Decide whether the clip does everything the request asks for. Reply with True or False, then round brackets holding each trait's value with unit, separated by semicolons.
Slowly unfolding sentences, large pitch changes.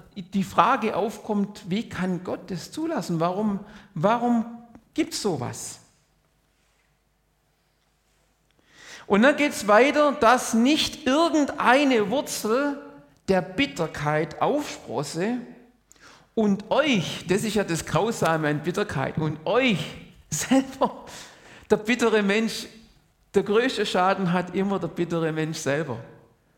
True (110 wpm; 5.9 semitones)